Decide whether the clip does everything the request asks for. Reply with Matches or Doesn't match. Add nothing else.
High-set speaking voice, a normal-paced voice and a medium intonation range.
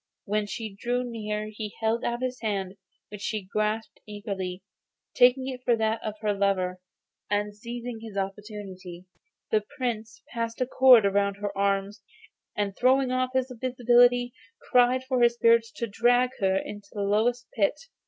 Matches